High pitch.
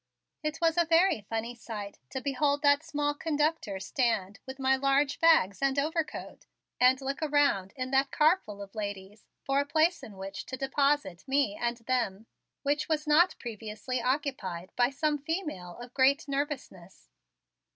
Yes: very high, 270 Hz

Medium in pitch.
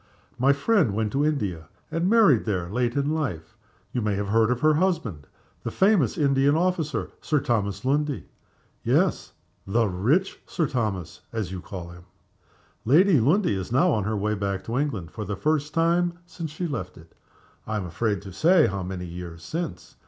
No: low, 120 Hz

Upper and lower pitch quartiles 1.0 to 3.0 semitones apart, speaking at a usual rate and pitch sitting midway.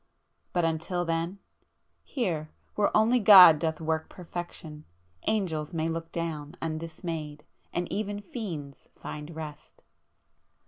No: narrow, 2.6 semitones; slow, 110 wpm; medium, 165 Hz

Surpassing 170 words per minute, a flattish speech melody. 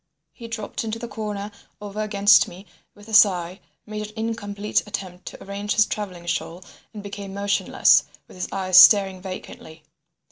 No: average, 165 wpm; narrow, 2.1 semitones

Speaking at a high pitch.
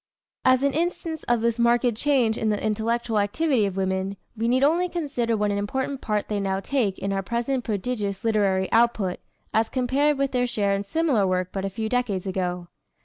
Yes: high, 225 Hz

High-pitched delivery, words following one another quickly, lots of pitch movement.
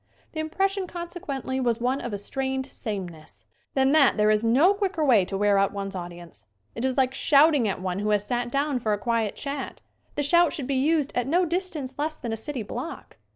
Yes: very high, 260 Hz; fast, 220 wpm; wide, 6.3 semitones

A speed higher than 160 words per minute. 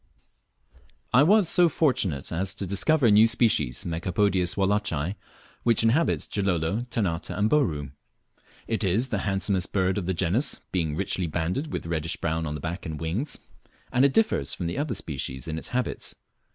Yes: average, 170 wpm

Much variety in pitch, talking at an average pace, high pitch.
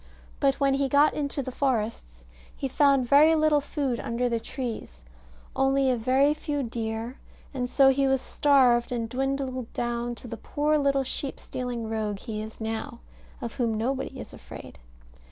No: average, 3.1 semitones; average, 170 wpm; very high, 255 Hz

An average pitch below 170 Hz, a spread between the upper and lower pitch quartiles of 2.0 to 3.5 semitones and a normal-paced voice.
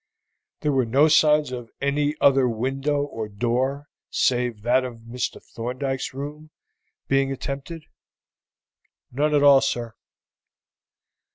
No: low, 135 Hz; average, 2.9 semitones; slow, 115 wpm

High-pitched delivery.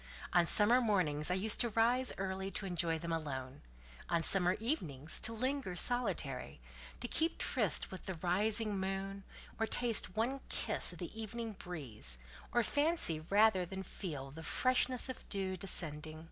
Yes: high, 195 Hz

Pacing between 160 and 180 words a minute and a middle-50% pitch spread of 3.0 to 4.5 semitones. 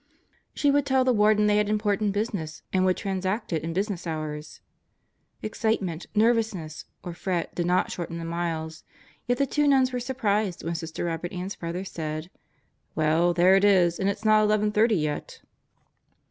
Yes: average, 175 wpm; average, 4.2 semitones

